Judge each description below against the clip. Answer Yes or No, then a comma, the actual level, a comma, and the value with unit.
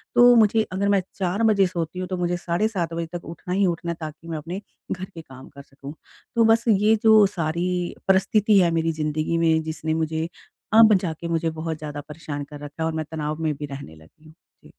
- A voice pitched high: No, medium, 165 Hz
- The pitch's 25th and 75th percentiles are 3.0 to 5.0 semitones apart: Yes, average, 3.6 semitones